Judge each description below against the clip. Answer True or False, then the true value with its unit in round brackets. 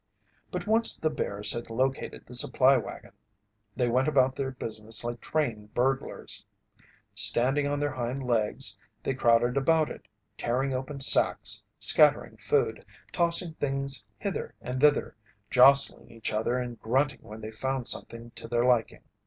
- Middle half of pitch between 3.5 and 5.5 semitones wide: False (2.7 semitones)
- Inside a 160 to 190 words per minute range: False (150 wpm)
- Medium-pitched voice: False (130 Hz)